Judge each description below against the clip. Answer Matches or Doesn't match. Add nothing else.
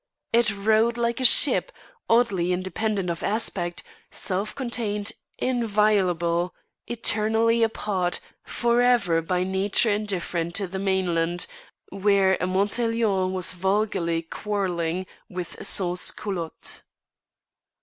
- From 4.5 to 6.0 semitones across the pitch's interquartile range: Doesn't match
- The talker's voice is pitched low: Doesn't match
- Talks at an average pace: Doesn't match